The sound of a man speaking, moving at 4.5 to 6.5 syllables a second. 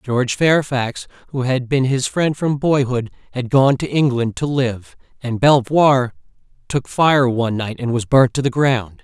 No: male; 4.3 syllables/s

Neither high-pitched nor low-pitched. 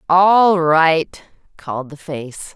Yes: medium, 165 Hz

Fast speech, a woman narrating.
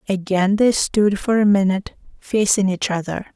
No: average, 160 wpm; female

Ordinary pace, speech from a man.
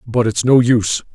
No: fast, 210 wpm; male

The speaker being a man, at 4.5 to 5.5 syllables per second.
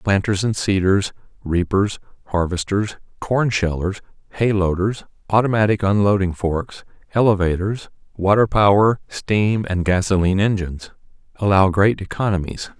Yes: male; 4.7 syllables/s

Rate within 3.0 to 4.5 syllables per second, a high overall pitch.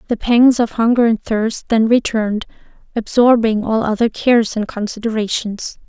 No: 4.9 syllables/s; high, 225 Hz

